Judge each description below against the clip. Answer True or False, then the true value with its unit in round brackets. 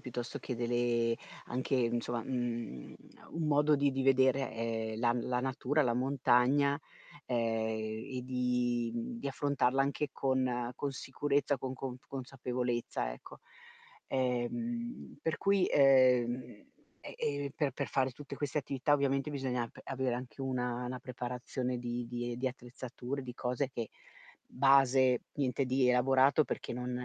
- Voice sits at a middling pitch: False (130 Hz)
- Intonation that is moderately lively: False (2.1 semitones)